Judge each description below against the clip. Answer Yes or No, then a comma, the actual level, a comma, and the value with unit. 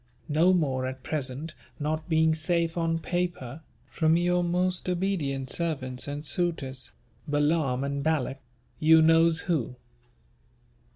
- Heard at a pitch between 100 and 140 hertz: No, medium, 160 Hz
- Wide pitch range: No, average, 3.5 semitones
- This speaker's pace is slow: Yes, slow, 120 wpm